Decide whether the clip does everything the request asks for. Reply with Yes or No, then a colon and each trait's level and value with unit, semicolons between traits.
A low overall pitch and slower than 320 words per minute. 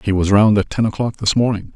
Yes: low, 105 Hz; fast, 275 wpm